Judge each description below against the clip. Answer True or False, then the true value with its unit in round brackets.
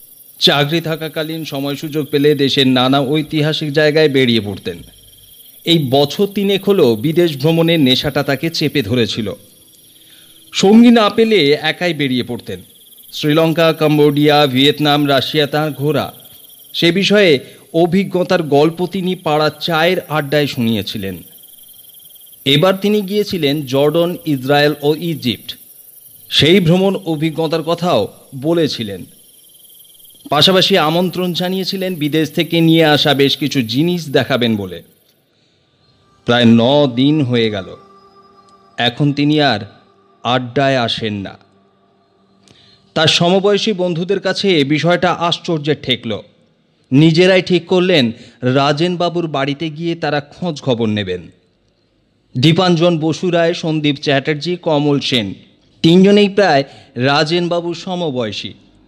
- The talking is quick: False (110 wpm)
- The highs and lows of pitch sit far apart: False (4.2 semitones)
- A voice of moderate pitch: True (150 Hz)